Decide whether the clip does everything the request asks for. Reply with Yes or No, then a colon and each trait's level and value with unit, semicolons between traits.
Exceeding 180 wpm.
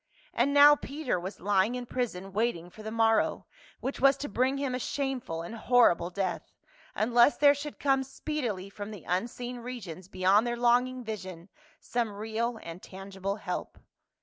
No: average, 165 wpm